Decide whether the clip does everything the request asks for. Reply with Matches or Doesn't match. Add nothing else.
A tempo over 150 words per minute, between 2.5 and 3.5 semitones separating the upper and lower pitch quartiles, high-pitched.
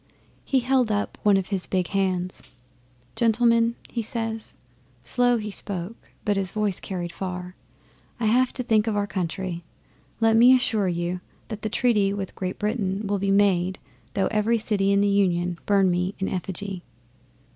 Matches